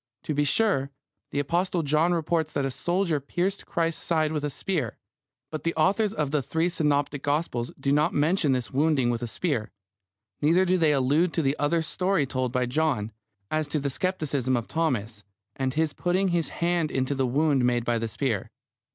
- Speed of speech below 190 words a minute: No, average, 195 wpm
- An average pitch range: Yes, average, 4.0 semitones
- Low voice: No, medium, 150 Hz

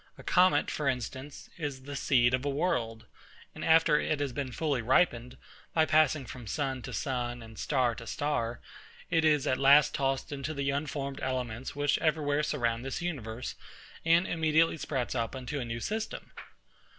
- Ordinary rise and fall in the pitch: Yes, average, 3.6 semitones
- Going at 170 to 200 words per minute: Yes, average, 175 wpm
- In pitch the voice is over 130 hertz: Yes, medium, 140 Hz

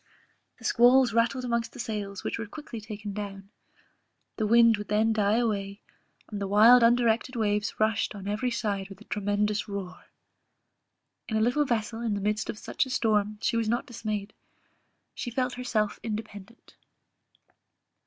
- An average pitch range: No, narrow, 2.3 semitones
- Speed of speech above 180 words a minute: No, average, 165 wpm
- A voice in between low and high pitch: No, high, 220 Hz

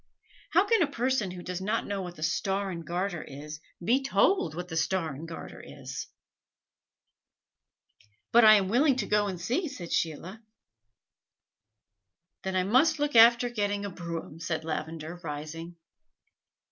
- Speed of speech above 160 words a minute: No, average, 155 wpm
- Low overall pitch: No, high, 190 Hz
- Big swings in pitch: Yes, wide, 5.8 semitones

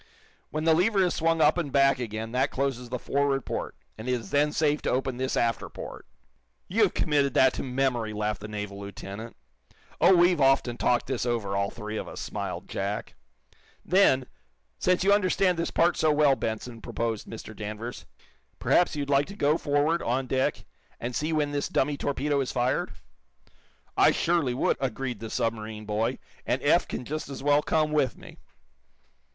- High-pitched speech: No, low, 135 Hz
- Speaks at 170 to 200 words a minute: Yes, average, 180 wpm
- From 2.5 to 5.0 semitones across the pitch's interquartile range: Yes, average, 4.7 semitones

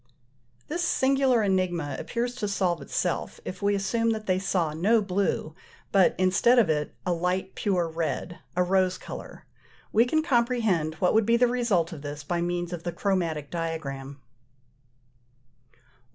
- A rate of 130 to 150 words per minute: No, average, 160 wpm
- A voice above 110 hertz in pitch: Yes, medium, 185 Hz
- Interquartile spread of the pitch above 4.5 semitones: Yes, average, 5.1 semitones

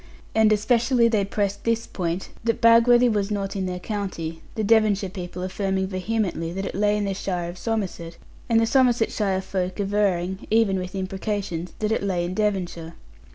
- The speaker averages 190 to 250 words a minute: No, average, 175 wpm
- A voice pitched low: No, high, 200 Hz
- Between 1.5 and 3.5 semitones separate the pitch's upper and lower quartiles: Yes, average, 3.0 semitones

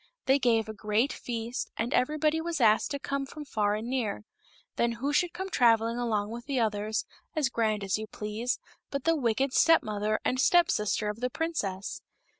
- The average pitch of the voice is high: Yes, high, 235 Hz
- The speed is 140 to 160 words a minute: No, average, 195 wpm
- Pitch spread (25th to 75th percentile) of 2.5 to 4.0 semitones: No, average, 4.5 semitones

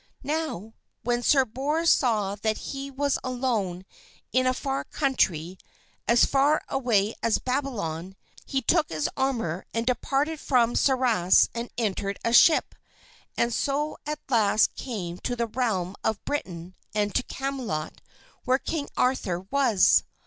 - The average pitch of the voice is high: Yes, high, 240 Hz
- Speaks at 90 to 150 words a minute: Yes, average, 140 wpm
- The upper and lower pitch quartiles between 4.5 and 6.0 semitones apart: Yes, average, 5.1 semitones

